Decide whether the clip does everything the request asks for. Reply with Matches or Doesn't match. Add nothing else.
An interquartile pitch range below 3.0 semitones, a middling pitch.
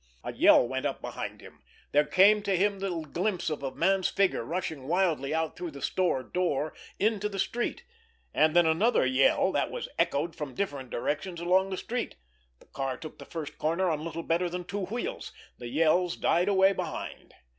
Doesn't match